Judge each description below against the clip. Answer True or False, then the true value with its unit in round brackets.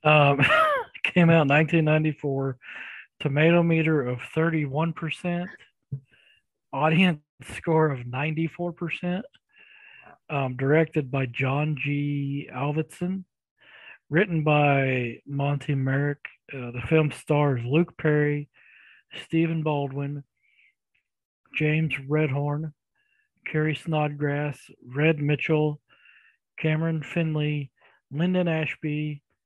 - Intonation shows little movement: True (2.3 semitones)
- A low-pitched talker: False (150 Hz)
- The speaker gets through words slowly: True (85 wpm)